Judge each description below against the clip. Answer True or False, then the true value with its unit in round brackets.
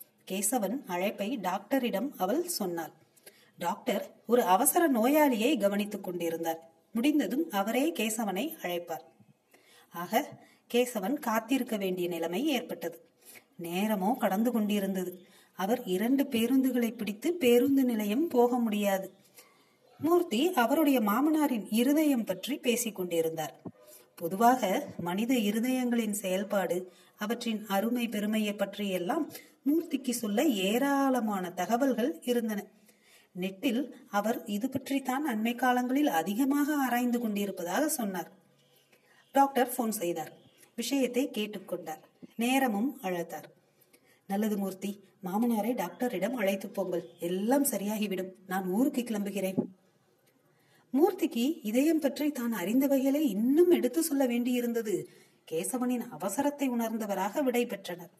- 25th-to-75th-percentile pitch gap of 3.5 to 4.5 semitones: False (5.3 semitones)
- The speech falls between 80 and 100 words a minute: True (90 wpm)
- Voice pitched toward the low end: False (230 Hz)